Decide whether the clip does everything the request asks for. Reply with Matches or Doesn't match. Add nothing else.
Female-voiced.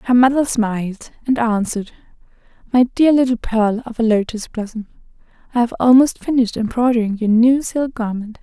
Matches